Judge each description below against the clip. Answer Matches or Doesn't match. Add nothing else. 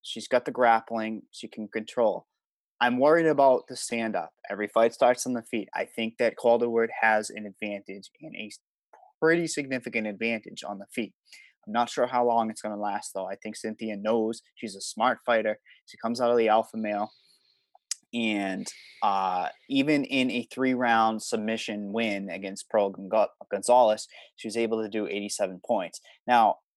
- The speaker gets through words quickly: Doesn't match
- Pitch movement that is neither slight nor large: Doesn't match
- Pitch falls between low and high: Doesn't match